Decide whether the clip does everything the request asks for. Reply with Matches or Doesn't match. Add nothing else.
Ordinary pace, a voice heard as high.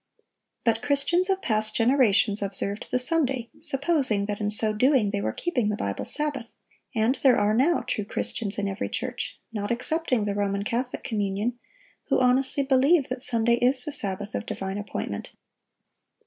Matches